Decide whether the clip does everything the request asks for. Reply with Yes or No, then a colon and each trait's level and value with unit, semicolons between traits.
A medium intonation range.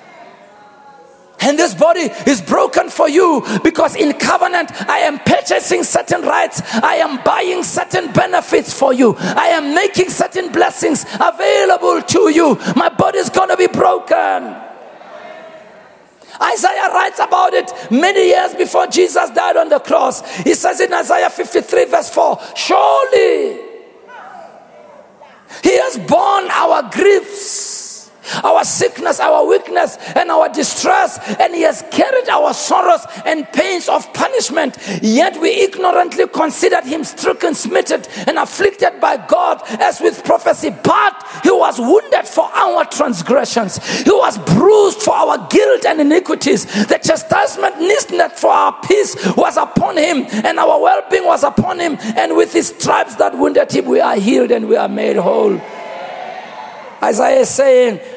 Yes: average, 4.7 semitones